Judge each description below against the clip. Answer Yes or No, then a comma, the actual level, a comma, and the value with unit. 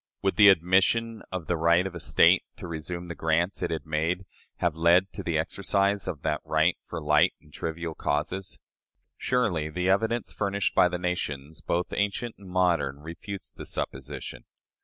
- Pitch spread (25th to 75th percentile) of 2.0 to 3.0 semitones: No, average, 3.4 semitones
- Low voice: Yes, very low, 85 Hz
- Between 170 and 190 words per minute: Yes, average, 175 wpm